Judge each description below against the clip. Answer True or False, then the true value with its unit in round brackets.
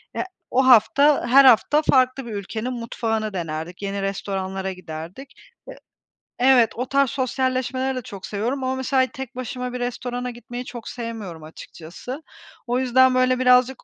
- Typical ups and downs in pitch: True (3.9 semitones)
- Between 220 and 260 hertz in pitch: True (245 Hz)